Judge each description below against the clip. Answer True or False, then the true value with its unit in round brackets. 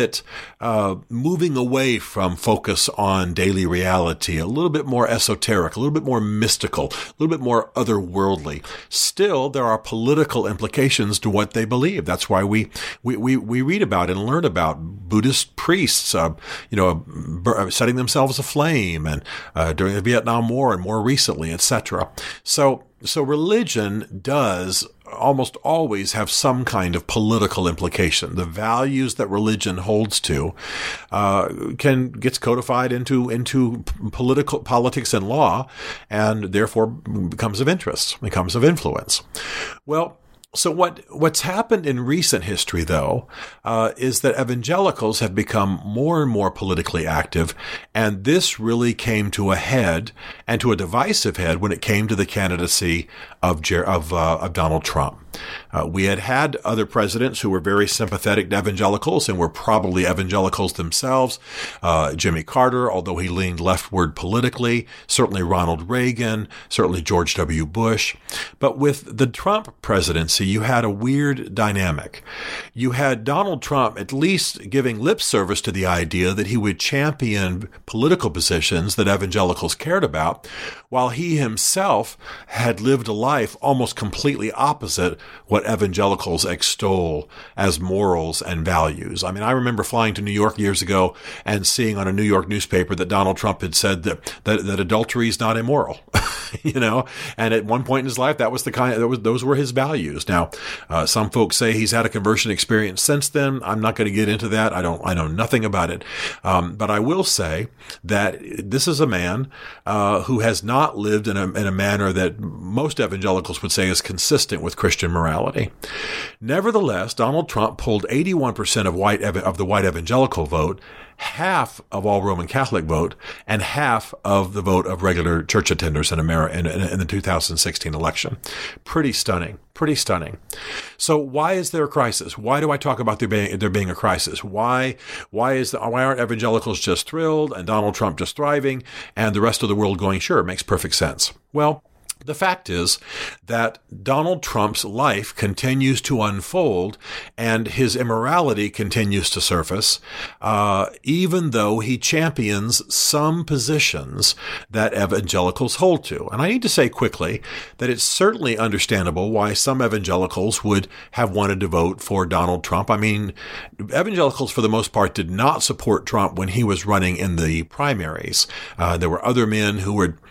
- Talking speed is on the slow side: False (170 wpm)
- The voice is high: False (110 Hz)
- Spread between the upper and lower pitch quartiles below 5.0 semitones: False (5.5 semitones)